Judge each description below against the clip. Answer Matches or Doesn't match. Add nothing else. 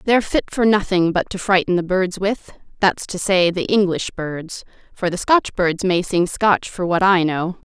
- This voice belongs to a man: Doesn't match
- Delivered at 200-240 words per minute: Matches